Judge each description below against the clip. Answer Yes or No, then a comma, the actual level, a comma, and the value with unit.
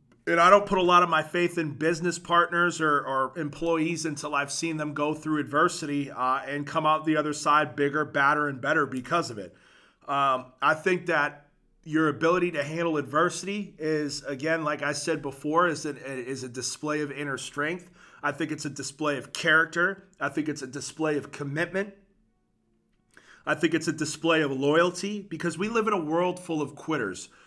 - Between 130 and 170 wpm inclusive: No, average, 195 wpm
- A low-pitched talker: No, medium, 155 Hz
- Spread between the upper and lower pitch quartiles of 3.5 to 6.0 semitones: No, average, 2.9 semitones